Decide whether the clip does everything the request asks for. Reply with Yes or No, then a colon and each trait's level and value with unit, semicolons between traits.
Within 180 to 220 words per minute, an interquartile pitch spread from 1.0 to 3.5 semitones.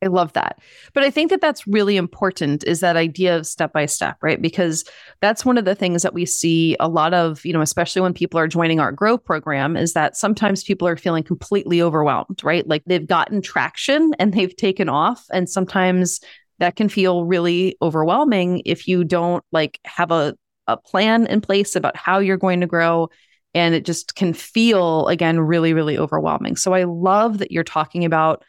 Yes: average, 200 wpm; average, 2.9 semitones